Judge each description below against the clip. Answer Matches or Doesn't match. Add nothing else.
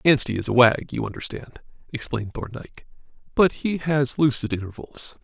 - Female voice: Doesn't match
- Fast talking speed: Doesn't match